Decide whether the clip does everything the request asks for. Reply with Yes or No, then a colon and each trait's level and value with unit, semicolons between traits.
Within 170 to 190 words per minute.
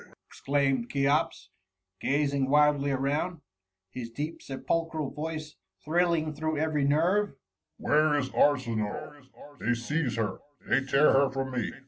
No: average, 140 wpm